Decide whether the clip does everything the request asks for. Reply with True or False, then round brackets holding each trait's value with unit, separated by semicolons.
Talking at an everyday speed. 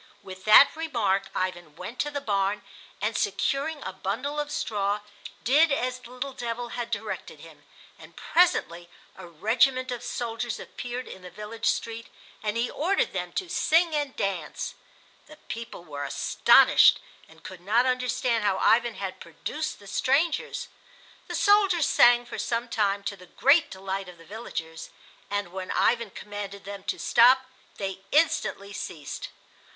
True (155 wpm)